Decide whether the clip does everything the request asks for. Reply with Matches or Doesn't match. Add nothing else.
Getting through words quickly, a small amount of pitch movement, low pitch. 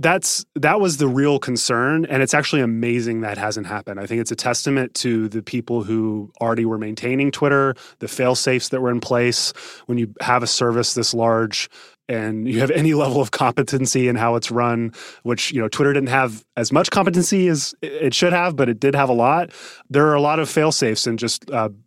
Doesn't match